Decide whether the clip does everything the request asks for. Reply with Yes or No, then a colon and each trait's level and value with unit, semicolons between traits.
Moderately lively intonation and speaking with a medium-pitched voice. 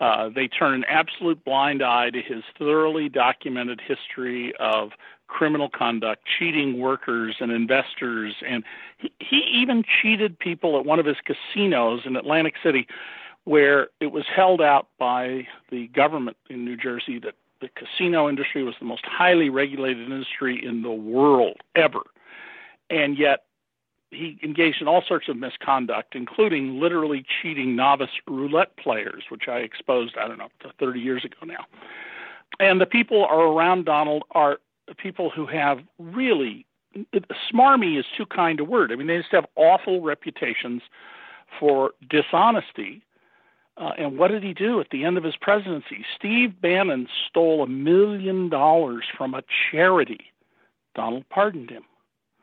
No: wide, 6.0 semitones; medium, 150 Hz